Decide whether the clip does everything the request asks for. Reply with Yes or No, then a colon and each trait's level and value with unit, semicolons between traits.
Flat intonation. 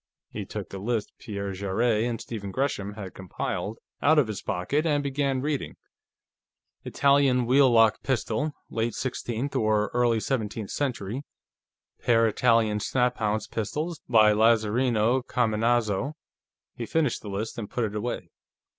No: average, 3.5 semitones